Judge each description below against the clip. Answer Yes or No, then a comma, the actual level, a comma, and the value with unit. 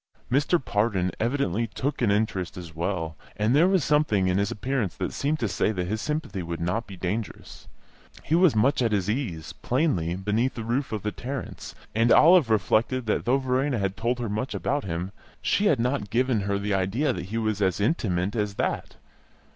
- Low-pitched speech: Yes, low, 110 Hz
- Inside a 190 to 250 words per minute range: Yes, average, 200 wpm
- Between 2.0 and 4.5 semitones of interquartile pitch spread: No, average, 5.2 semitones